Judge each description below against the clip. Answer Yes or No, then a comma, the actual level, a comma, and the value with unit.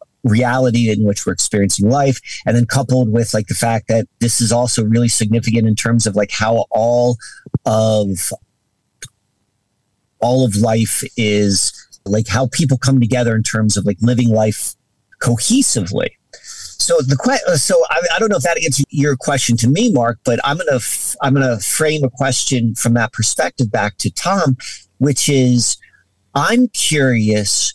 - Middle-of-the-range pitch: No, low, 120 Hz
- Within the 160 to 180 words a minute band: Yes, average, 165 wpm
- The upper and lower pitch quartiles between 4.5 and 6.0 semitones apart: No, average, 3.2 semitones